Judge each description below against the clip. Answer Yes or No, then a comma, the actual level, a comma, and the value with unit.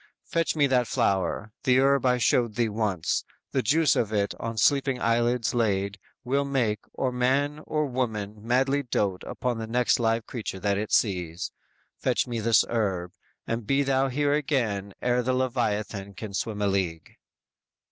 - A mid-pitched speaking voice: No, low, 115 Hz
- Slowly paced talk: No, average, 165 wpm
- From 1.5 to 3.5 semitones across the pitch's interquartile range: No, average, 4.2 semitones